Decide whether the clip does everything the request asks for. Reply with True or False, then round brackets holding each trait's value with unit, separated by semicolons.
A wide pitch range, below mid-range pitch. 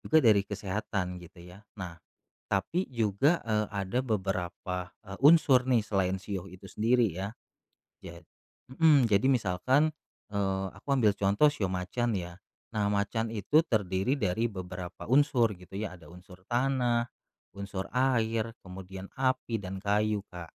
False (4.3 semitones; 100 Hz)